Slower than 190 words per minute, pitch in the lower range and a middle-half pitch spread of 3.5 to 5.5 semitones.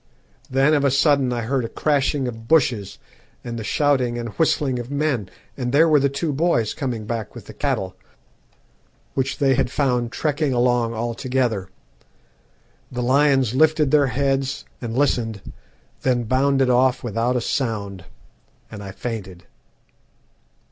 No: average, 150 wpm; low, 125 Hz; average, 3.1 semitones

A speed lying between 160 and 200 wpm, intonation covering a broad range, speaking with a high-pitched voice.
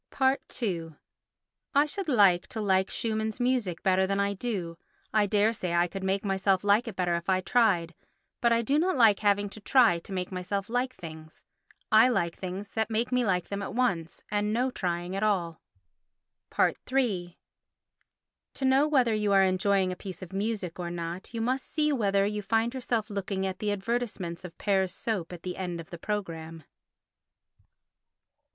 No: average, 180 wpm; average, 3.9 semitones; high, 200 Hz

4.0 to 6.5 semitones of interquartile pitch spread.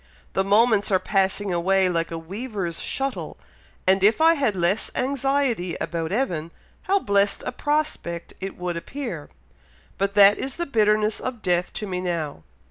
Yes: wide, 5.6 semitones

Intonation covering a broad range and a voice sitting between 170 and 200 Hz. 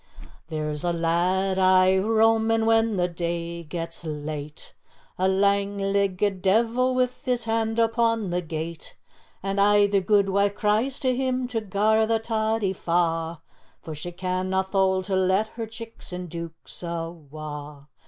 No: average, 4.6 semitones; high, 190 Hz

